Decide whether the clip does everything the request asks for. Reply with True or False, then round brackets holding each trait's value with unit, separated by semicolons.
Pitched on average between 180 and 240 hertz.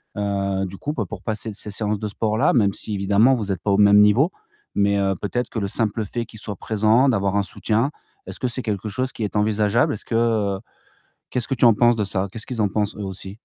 False (105 Hz)